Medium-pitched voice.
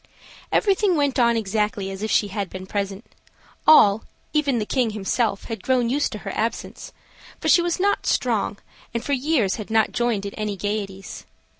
No: high, 220 Hz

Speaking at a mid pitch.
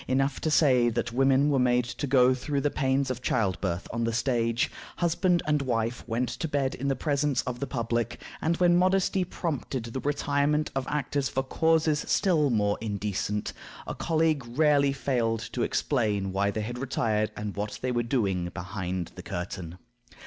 No: low, 130 Hz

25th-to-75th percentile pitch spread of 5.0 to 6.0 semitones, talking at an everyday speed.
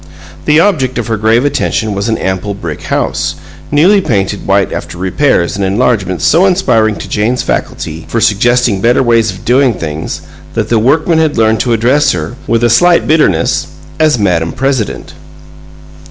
Yes: wide, 5.4 semitones; average, 170 wpm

